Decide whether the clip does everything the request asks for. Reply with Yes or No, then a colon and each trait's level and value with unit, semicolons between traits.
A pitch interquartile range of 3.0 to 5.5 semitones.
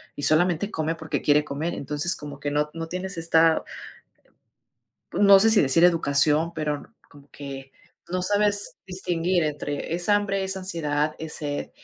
Yes: average, 3.7 semitones